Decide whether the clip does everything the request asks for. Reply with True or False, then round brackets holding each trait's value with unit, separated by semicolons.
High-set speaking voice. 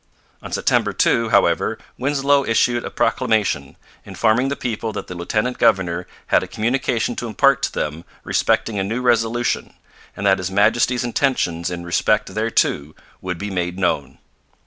False (110 Hz)